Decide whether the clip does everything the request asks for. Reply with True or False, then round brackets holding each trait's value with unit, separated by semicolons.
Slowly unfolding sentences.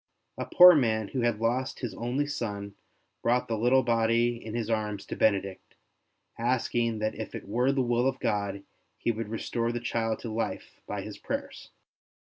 False (180 wpm)